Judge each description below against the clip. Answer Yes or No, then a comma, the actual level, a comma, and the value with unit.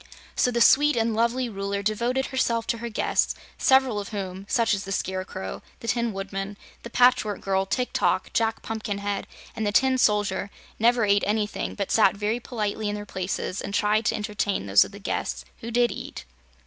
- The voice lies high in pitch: Yes, high, 215 Hz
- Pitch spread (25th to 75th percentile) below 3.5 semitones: Yes, average, 2.8 semitones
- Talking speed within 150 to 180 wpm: No, average, 190 wpm